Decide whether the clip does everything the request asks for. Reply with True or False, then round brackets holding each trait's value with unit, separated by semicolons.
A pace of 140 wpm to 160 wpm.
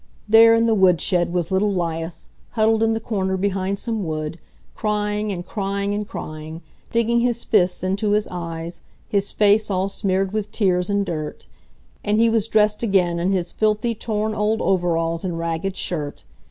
False (170 wpm)